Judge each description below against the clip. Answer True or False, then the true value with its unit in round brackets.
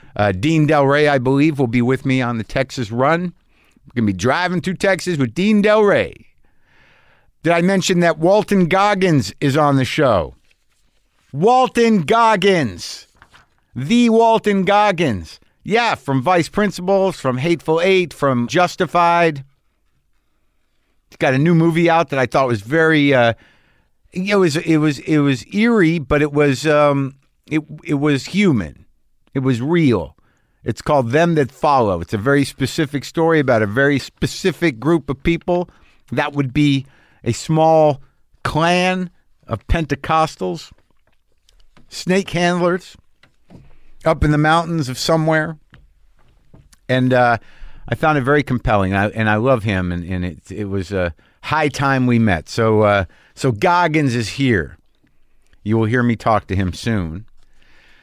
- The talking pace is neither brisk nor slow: True (155 wpm)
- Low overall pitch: False (145 Hz)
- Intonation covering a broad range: True (6.1 semitones)